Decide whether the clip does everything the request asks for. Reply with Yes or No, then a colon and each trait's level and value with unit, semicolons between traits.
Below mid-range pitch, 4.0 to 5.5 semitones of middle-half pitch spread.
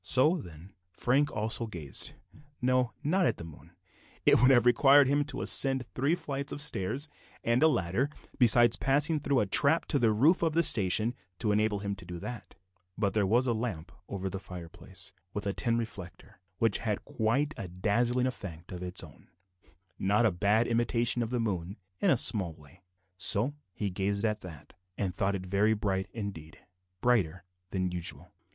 Yes: low, 110 Hz; average, 5.0 semitones